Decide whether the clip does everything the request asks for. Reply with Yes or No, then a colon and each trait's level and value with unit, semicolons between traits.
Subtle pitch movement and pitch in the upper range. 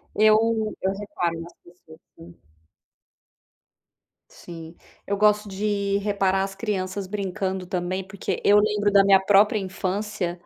Yes: narrow, 2.0 semitones; high, 195 Hz